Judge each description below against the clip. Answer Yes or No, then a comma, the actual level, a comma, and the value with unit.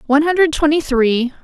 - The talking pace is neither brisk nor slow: Yes, average, 170 wpm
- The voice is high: Yes, very high, 290 Hz